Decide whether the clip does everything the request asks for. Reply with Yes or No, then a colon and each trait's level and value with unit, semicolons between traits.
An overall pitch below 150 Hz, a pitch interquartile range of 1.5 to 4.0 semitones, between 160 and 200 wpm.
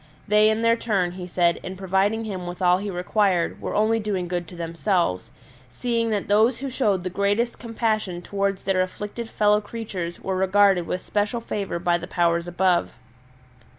No: high, 195 Hz; average, 3.2 semitones; average, 180 wpm